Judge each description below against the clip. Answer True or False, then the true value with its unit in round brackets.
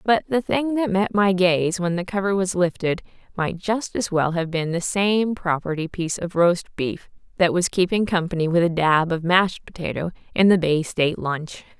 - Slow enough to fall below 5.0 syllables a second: True (4.8 syllables/s)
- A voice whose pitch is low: False (180 Hz)